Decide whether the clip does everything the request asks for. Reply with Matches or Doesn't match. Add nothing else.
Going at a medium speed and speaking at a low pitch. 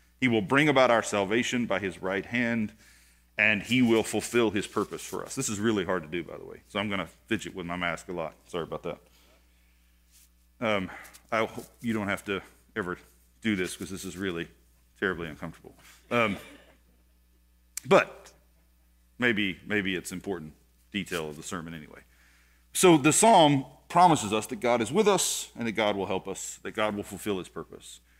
Matches